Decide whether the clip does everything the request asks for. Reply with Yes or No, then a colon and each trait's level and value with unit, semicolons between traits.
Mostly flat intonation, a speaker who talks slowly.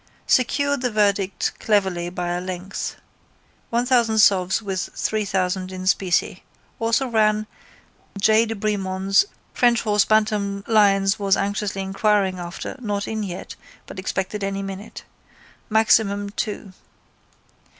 Yes: narrow, 2.3 semitones; slow, 120 wpm